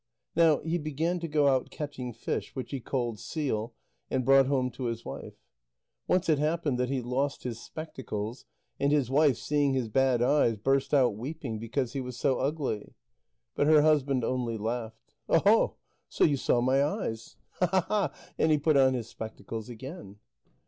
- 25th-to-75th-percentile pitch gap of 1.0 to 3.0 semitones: No, average, 3.7 semitones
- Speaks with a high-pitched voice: No, low, 135 Hz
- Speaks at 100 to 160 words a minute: No, average, 175 wpm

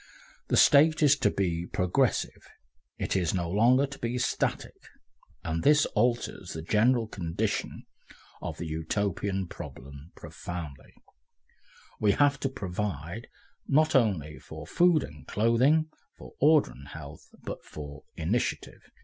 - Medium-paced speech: No, slow, 130 wpm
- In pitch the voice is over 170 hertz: No, low, 100 Hz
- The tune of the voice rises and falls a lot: Yes, wide, 8.2 semitones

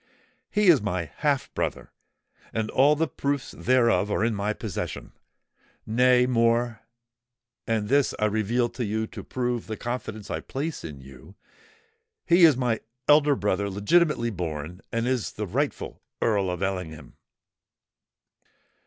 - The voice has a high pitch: No, low, 115 Hz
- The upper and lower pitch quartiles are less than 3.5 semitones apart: No, average, 4.0 semitones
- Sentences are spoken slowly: Yes, slow, 130 wpm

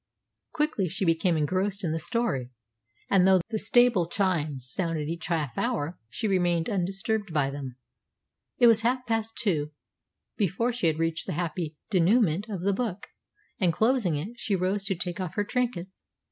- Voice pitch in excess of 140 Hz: Yes, medium, 185 Hz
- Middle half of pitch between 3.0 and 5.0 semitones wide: Yes, average, 4.7 semitones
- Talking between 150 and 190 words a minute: Yes, average, 170 wpm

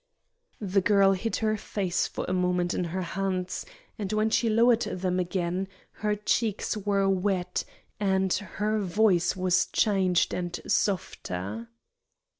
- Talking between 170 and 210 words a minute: No, slow, 135 wpm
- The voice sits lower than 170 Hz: No, high, 190 Hz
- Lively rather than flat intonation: No, narrow, 2.6 semitones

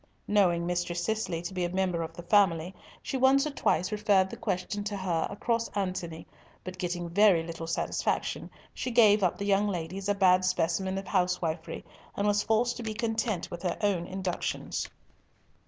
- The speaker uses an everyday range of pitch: Yes, average, 3.1 semitones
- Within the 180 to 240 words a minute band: Yes, average, 185 wpm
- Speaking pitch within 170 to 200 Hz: Yes, high, 190 Hz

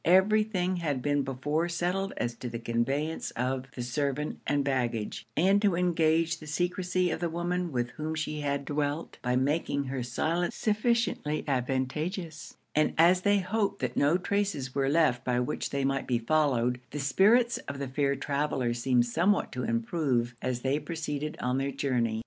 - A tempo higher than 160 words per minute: Yes, average, 175 wpm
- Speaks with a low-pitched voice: No, medium, 145 Hz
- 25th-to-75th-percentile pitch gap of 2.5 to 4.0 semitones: No, average, 5.1 semitones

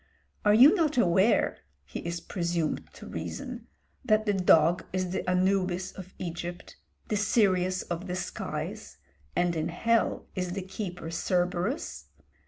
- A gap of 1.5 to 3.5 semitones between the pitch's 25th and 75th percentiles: Yes, average, 2.8 semitones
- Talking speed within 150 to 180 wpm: No, average, 140 wpm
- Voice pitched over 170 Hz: Yes, medium, 185 Hz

